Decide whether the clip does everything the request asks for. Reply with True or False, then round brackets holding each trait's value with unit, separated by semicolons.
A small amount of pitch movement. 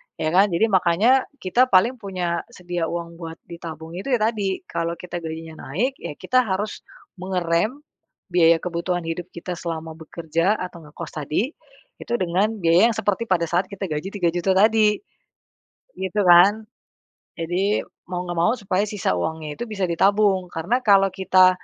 False (3.3 semitones)